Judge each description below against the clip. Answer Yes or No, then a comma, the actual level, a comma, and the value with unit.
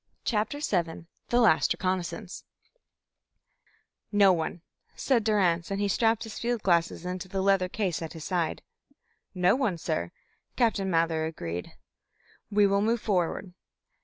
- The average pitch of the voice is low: No, high, 190 Hz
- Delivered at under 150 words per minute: Yes, slow, 135 wpm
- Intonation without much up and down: No, average, 3.8 semitones